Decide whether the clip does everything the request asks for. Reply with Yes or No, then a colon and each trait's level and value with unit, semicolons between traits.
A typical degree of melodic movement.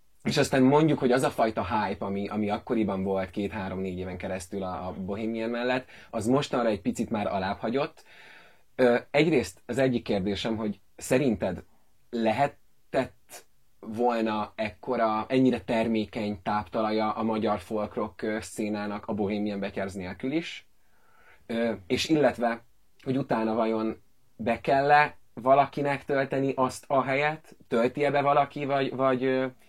Yes: average, 4.0 semitones